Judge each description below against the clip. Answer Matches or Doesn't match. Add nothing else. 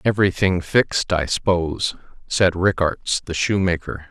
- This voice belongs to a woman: Doesn't match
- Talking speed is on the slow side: Matches